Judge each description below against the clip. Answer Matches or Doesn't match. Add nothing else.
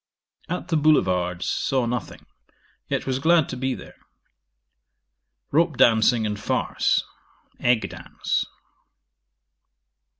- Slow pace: Matches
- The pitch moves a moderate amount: Doesn't match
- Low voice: Matches